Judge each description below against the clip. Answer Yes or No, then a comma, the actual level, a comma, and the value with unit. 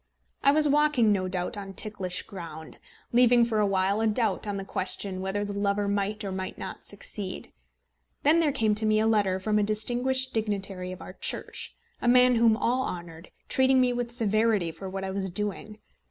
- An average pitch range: Yes, average, 3.6 semitones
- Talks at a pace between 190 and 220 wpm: Yes, average, 200 wpm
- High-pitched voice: Yes, high, 210 Hz